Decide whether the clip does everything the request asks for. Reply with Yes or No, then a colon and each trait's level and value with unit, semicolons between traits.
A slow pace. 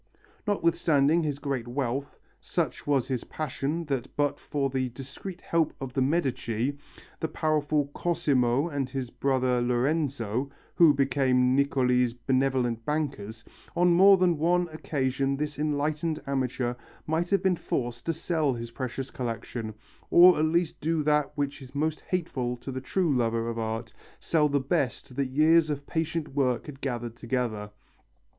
No: average, 150 wpm